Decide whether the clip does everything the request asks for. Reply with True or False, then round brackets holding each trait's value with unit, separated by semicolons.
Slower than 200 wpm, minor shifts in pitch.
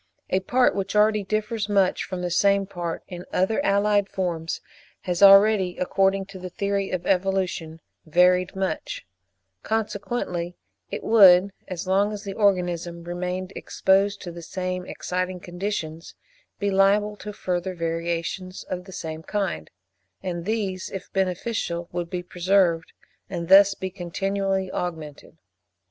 True (140 wpm; 2.2 semitones)